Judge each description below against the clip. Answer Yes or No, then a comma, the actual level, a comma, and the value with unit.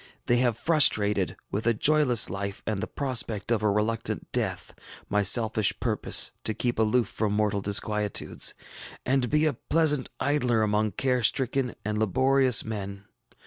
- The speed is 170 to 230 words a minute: No, average, 150 wpm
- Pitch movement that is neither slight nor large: Yes, average, 3.7 semitones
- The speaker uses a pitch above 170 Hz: No, low, 110 Hz